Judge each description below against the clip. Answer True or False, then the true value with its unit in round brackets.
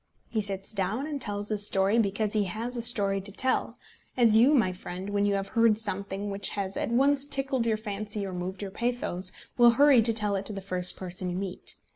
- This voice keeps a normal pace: False (225 wpm)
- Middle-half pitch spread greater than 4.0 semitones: False (3.0 semitones)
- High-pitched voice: True (205 Hz)